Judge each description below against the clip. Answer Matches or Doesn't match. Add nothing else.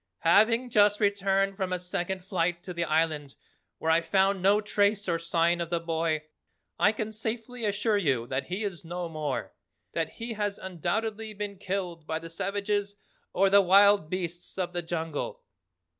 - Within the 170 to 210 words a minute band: Matches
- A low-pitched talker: Doesn't match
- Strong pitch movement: Doesn't match